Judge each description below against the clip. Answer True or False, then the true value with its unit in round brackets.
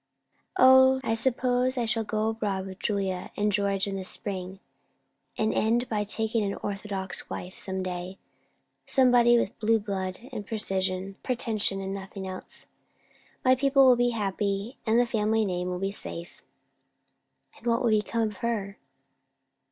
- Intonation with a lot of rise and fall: False (3.4 semitones)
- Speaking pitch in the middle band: False (210 Hz)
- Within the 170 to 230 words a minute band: False (150 wpm)